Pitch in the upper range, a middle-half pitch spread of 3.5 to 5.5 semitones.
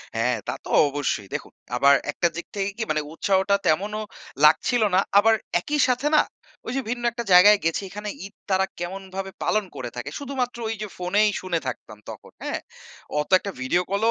Yes: high, 195 Hz; average, 4.6 semitones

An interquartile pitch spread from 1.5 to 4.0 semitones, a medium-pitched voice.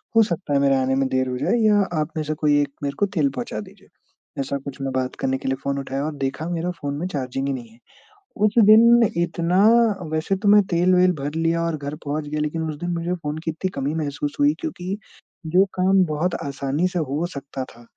No: average, 4.4 semitones; medium, 150 Hz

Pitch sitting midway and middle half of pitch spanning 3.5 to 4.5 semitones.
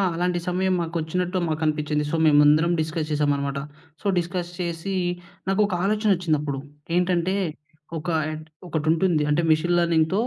No: medium, 165 Hz; average, 2.8 semitones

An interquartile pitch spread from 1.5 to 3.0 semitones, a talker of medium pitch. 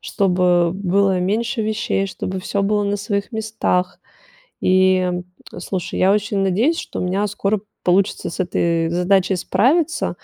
No: narrow, 2.4 semitones; high, 195 Hz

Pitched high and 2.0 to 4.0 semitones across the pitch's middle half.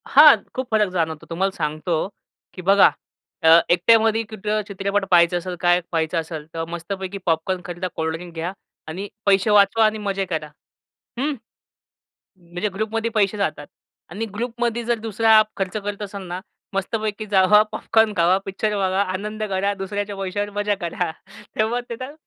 Yes: high, 195 Hz; average, 3.4 semitones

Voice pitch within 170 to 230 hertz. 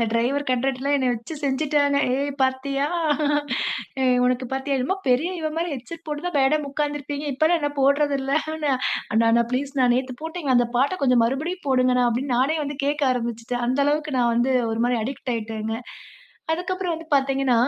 No: very high, 275 Hz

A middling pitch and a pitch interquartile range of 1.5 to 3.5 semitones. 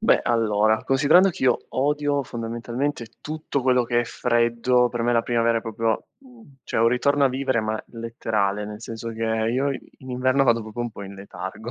No: low, 120 Hz; narrow, 2.6 semitones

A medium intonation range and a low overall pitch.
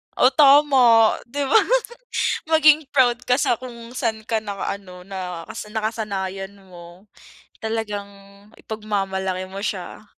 No: average, 4.3 semitones; high, 220 Hz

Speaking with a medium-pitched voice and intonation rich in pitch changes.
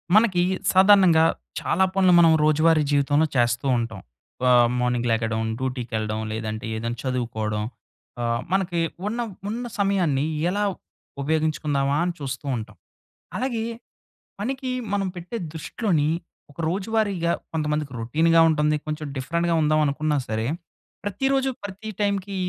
Yes: medium, 155 Hz; wide, 7.3 semitones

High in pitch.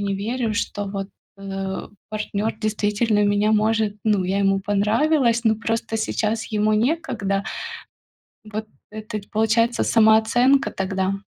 Yes: high, 215 Hz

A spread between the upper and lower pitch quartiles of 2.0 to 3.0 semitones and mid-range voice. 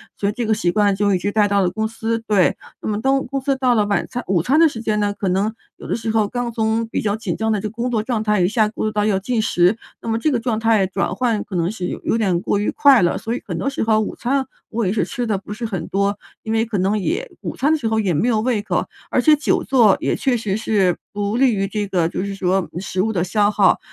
No: average, 2.7 semitones; high, 215 Hz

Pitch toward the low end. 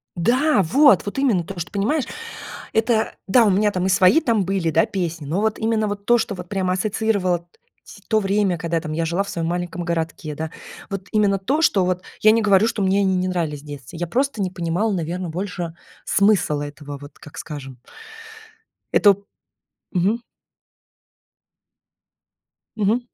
No: high, 190 Hz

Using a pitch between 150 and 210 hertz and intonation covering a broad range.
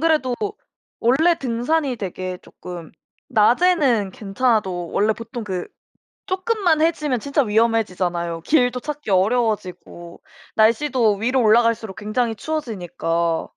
No: high, 230 Hz; wide, 5.8 semitones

